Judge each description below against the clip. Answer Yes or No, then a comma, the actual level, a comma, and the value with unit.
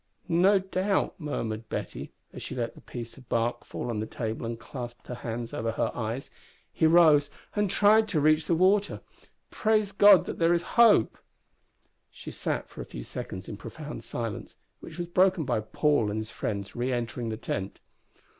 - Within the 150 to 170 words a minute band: No, average, 185 wpm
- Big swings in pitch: Yes, wide, 7.7 semitones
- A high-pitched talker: No, medium, 140 Hz